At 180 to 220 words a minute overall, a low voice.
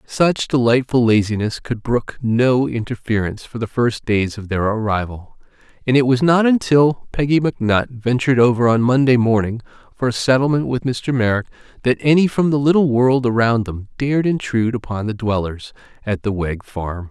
No: average, 170 wpm; low, 120 Hz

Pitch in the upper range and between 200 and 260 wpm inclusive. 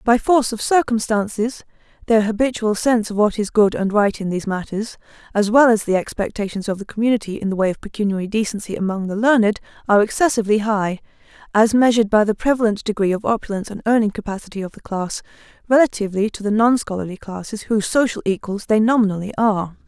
No: high, 215 Hz; average, 185 wpm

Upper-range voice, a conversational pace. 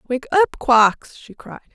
Yes: very high, 260 Hz; average, 170 wpm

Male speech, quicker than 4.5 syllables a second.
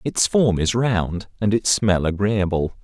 No: male; 3.9 syllables/s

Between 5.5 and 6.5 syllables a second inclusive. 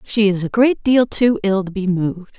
No: 4.9 syllables/s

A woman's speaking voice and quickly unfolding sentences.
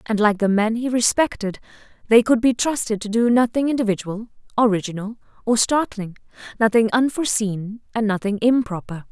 No: female; average, 140 wpm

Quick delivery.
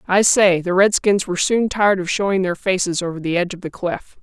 Yes: fast, 240 wpm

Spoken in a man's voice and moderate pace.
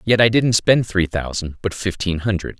No: male; fast, 210 wpm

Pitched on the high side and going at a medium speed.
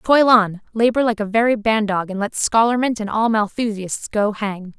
Yes: high, 220 Hz; average, 190 wpm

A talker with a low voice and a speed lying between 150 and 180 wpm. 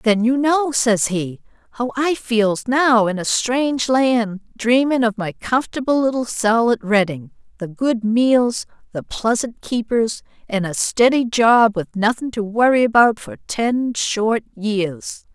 No: high, 230 Hz; average, 155 wpm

